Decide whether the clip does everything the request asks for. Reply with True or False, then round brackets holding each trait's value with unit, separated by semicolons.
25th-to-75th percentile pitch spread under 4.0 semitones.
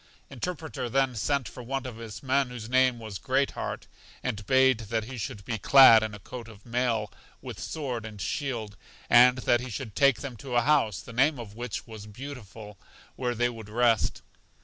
True (3.1 semitones)